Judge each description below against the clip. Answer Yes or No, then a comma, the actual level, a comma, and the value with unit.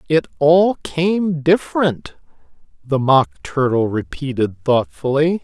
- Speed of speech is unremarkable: No, slow, 100 wpm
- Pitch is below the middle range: No, medium, 145 Hz